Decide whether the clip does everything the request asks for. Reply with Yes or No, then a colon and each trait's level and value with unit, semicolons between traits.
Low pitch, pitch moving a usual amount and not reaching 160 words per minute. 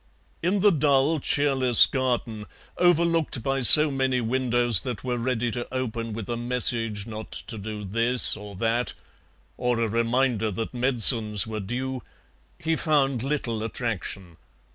Yes: low, 120 Hz; average, 3.0 semitones; average, 140 wpm